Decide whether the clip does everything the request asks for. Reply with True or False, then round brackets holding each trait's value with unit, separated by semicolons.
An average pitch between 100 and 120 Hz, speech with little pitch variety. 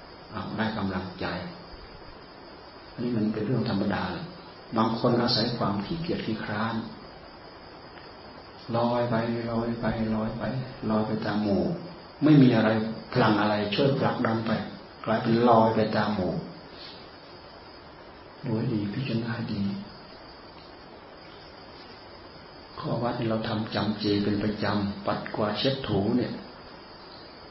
True (110 Hz; 1.9 semitones)